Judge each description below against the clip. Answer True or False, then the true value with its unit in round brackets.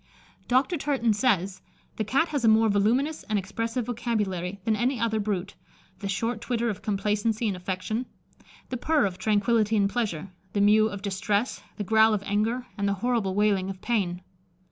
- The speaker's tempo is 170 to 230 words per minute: True (175 wpm)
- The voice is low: False (215 Hz)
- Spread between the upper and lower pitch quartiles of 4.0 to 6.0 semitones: False (2.9 semitones)